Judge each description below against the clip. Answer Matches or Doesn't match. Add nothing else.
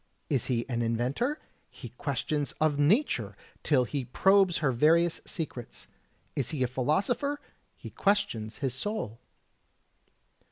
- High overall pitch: Doesn't match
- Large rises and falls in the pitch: Matches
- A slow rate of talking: Matches